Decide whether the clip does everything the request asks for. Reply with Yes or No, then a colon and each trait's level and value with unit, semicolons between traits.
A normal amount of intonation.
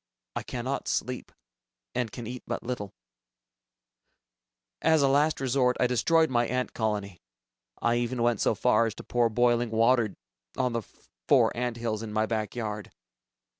No: narrow, 2.2 semitones